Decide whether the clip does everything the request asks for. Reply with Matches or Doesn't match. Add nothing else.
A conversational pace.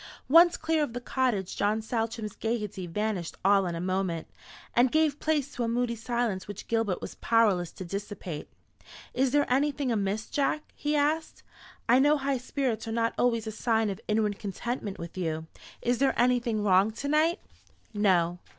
Matches